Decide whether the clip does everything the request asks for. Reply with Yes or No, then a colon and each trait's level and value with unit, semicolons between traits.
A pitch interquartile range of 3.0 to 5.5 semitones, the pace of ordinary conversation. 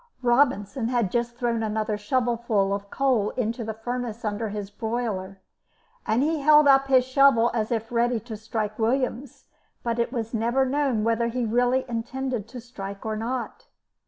No: narrow, 2.6 semitones; average, 165 wpm